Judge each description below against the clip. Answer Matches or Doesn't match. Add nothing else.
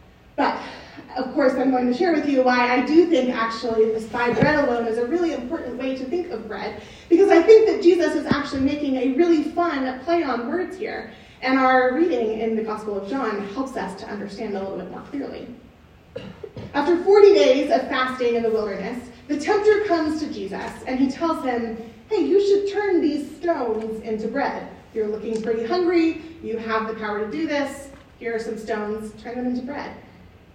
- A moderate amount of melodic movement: Doesn't match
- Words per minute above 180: Matches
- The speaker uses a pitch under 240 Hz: Doesn't match